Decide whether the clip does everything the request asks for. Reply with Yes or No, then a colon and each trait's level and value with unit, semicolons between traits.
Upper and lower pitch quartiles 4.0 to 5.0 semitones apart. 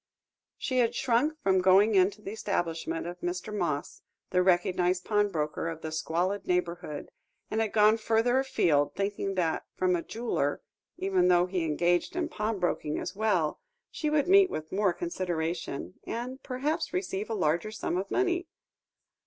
Yes: average, 4.3 semitones